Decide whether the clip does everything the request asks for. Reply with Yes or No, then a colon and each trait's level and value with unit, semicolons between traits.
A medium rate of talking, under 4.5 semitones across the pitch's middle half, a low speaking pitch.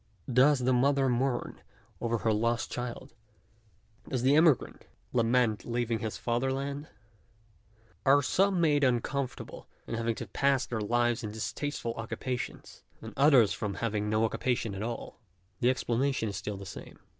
Yes: average, 155 wpm; average, 3.0 semitones; low, 120 Hz